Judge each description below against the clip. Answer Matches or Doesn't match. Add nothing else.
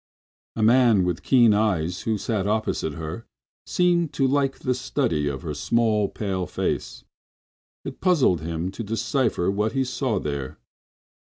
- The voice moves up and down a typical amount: Doesn't match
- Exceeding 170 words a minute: Doesn't match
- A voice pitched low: Matches